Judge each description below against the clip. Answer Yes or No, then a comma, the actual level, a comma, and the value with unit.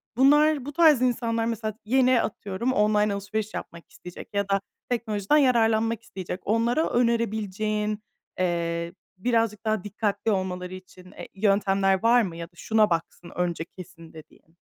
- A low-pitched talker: No, high, 210 Hz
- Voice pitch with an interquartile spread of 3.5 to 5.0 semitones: Yes, average, 3.8 semitones